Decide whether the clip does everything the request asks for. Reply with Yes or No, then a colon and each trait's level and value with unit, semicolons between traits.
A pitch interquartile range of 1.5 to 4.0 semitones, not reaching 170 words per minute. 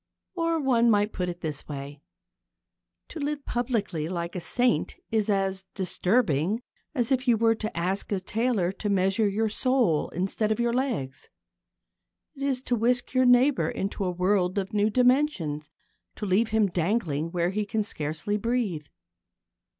No: average, 5.2 semitones; average, 160 wpm